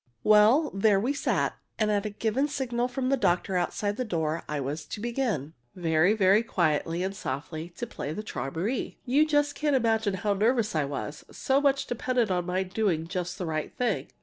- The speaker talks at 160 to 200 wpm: Yes, average, 195 wpm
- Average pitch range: No, wide, 6.1 semitones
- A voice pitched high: Yes, high, 205 Hz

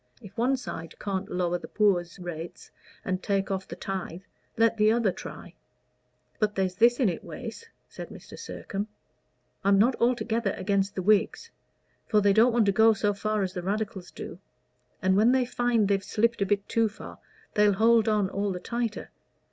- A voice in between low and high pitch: No, high, 205 Hz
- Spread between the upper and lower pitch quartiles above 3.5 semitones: No, average, 2.8 semitones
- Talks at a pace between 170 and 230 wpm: Yes, average, 185 wpm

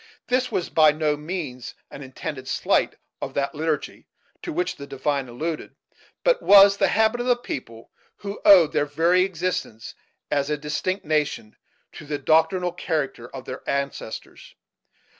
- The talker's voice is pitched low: No, medium, 155 Hz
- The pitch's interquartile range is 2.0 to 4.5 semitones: No, average, 4.9 semitones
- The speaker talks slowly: No, average, 155 wpm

